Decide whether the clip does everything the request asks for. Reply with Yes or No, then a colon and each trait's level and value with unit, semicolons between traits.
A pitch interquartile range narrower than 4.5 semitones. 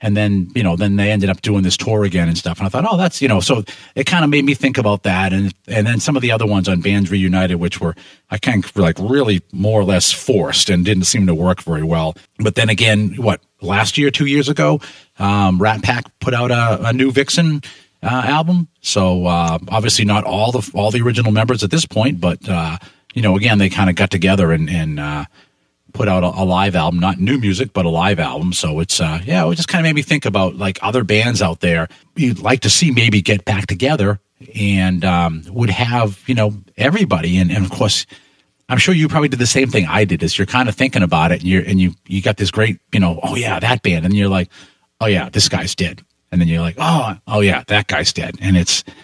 No: average, 5.0 semitones